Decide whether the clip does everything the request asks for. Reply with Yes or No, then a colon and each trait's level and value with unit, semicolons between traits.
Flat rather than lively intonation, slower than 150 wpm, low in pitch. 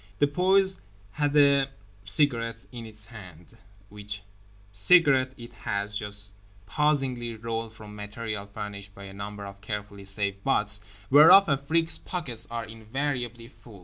No: average, 5.1 semitones; slow, 135 wpm; low, 115 Hz